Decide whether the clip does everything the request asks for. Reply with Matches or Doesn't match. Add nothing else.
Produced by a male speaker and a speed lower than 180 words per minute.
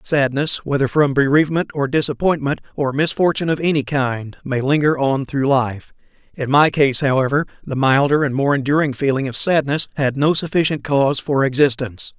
Matches